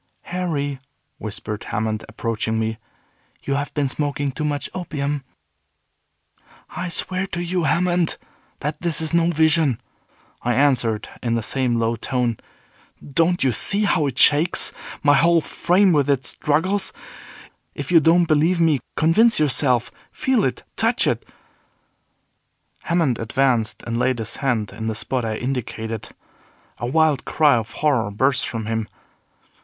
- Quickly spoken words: No, average, 145 wpm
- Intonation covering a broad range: Yes, wide, 5.8 semitones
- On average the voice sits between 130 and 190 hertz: Yes, medium, 140 Hz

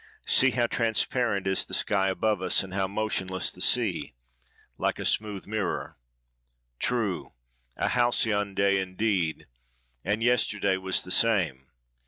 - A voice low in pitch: Yes, low, 100 Hz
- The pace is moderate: No, slow, 130 wpm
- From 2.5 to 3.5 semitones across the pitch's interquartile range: Yes, average, 2.9 semitones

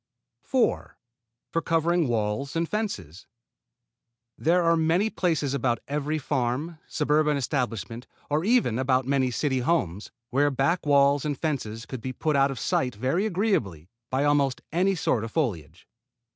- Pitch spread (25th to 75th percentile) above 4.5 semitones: Yes, average, 5.0 semitones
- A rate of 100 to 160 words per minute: Yes, average, 145 wpm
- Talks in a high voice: No, medium, 140 Hz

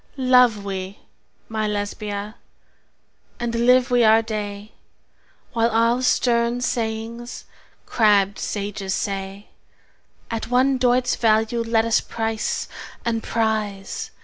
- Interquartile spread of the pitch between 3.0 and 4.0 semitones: No, narrow, 2.4 semitones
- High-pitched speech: Yes, high, 225 Hz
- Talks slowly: Yes, slow, 105 wpm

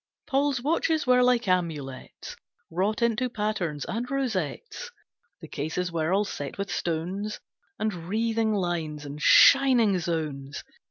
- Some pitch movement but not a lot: No, wide, 6.7 semitones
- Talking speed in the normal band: No, slow, 125 wpm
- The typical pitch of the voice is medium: No, high, 195 Hz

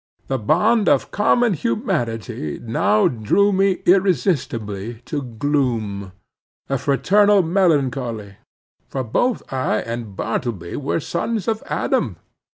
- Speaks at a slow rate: Yes, slow, 115 wpm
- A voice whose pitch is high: No, low, 135 Hz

